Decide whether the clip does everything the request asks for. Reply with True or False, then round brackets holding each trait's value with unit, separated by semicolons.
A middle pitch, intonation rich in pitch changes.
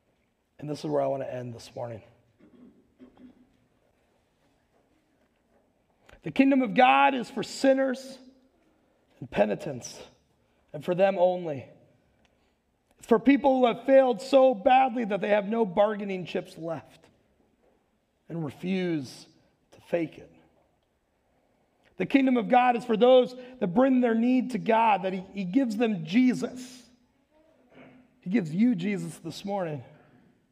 False (225 Hz; 6.4 semitones)